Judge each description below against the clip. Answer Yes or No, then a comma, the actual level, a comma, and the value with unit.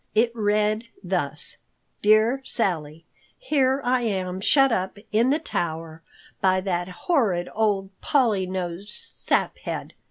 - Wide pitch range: No, average, 4.5 semitones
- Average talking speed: No, slow, 120 wpm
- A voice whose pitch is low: No, high, 210 Hz